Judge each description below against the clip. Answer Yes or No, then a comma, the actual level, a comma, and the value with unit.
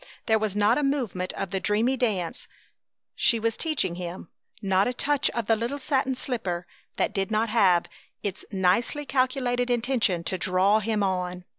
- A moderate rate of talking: Yes, average, 170 wpm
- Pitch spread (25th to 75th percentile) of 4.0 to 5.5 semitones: Yes, average, 4.8 semitones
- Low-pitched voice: No, high, 215 Hz